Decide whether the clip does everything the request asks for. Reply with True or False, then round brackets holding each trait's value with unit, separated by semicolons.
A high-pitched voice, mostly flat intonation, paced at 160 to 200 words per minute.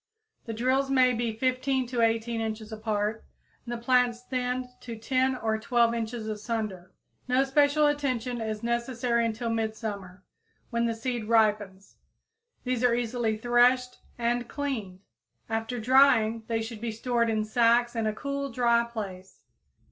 False (235 Hz; 2.2 semitones; 150 wpm)